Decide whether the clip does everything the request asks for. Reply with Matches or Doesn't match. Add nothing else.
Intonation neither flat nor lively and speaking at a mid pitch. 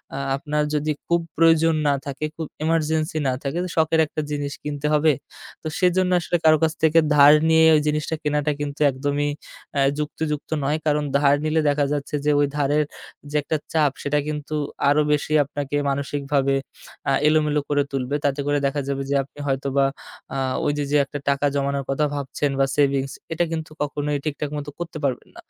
Doesn't match